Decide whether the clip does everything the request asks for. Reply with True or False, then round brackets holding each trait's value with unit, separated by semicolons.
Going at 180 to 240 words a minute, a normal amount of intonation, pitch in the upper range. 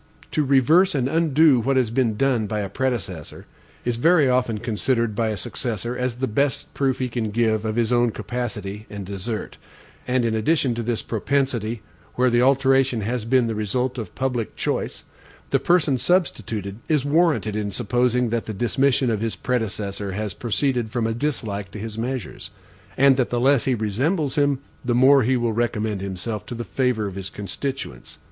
False (185 wpm; 3.5 semitones; 120 Hz)